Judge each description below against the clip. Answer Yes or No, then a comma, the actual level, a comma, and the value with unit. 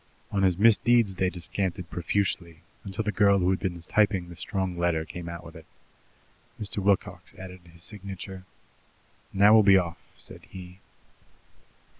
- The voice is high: No, very low, 95 Hz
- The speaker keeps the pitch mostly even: Yes, narrow, 2.3 semitones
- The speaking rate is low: No, average, 155 wpm